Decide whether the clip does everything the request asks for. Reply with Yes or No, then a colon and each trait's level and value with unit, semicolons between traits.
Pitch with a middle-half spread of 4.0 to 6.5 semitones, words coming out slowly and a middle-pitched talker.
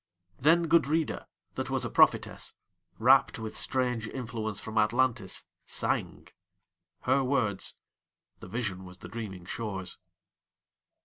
No: average, 5.3 semitones; slow, 105 wpm; low, 110 Hz